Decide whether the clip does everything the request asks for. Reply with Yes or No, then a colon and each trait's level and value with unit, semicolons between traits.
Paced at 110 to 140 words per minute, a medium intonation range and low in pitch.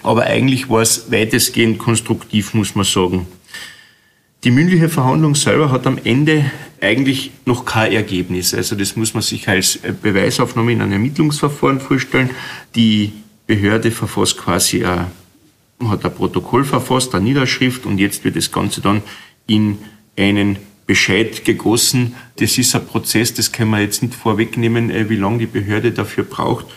No: average, 150 wpm; average, 3.7 semitones; low, 115 Hz